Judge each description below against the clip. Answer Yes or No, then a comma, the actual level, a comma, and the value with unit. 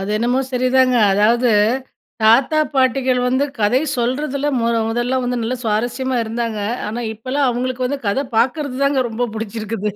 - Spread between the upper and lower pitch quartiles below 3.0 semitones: Yes, narrow, 2.4 semitones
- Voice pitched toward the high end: Yes, high, 245 Hz